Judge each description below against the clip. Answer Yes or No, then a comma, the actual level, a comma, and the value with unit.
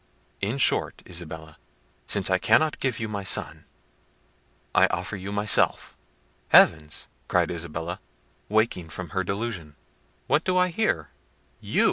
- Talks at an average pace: No, slow, 130 wpm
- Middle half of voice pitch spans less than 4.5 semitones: No, average, 4.9 semitones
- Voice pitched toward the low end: Yes, low, 100 Hz